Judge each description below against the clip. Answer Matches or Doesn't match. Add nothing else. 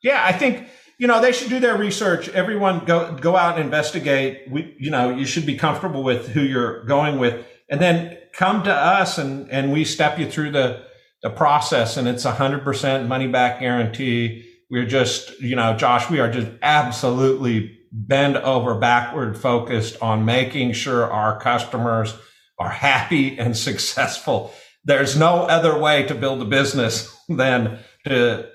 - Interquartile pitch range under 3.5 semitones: Doesn't match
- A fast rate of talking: Doesn't match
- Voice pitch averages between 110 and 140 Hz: Matches